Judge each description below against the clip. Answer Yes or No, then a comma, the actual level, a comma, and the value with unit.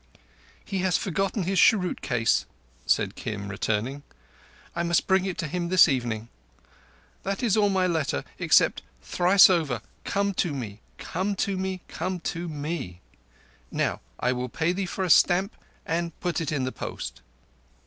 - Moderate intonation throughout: No, wide, 6.2 semitones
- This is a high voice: No, medium, 170 Hz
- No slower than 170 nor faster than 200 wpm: No, average, 160 wpm